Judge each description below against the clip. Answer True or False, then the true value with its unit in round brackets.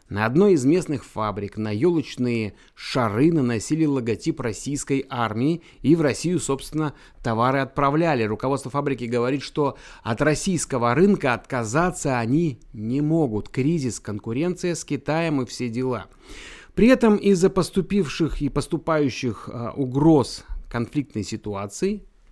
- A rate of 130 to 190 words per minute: False (120 wpm)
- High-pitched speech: False (135 Hz)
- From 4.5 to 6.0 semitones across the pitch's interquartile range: True (5.4 semitones)